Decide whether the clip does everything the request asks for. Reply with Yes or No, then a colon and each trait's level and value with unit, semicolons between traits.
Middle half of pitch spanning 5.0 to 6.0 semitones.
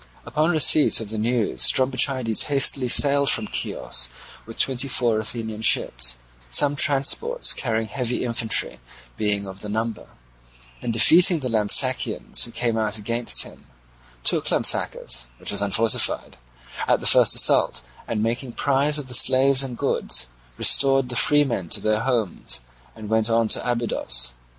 No: average, 3.7 semitones